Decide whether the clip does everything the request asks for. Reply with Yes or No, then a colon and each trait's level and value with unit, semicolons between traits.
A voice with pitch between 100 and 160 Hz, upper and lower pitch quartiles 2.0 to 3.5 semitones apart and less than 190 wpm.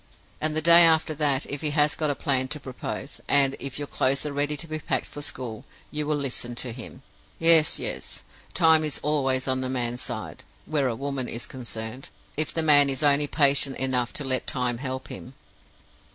No: medium, 140 Hz; narrow, 2.5 semitones; fast, 205 wpm